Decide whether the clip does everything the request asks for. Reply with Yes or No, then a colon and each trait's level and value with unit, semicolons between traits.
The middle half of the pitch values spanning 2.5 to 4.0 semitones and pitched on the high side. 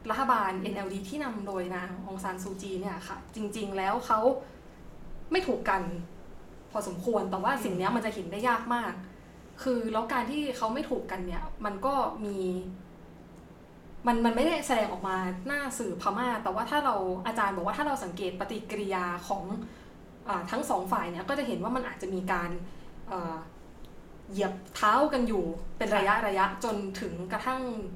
No: average, 4.4 semitones; high, 205 Hz